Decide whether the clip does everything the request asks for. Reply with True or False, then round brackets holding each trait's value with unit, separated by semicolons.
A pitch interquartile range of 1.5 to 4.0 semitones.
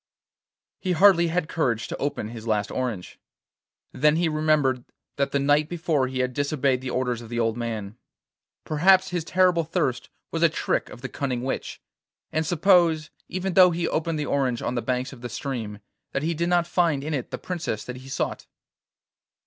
False (5.0 semitones)